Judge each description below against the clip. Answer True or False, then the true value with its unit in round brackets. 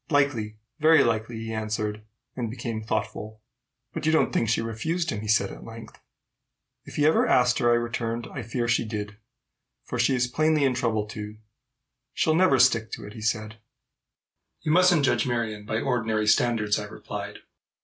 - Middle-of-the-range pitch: False (115 Hz)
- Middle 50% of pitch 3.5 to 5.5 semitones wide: False (3.1 semitones)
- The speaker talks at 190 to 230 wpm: False (180 wpm)